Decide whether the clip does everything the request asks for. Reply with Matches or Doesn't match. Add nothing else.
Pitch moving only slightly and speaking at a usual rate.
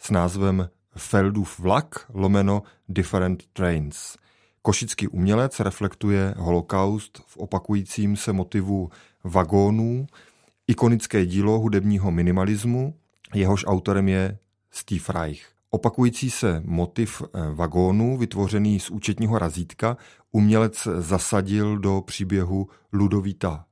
Doesn't match